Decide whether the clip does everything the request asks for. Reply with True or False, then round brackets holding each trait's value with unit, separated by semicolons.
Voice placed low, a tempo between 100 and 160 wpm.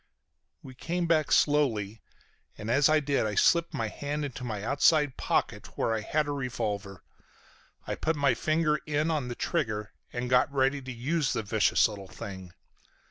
False (130 Hz; 180 wpm)